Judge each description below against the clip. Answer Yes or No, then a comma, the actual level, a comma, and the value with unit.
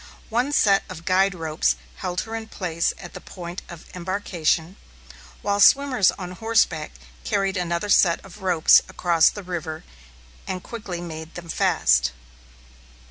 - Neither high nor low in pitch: Yes, medium, 180 Hz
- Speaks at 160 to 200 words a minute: No, average, 140 wpm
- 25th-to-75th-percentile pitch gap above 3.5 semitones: No, average, 3.1 semitones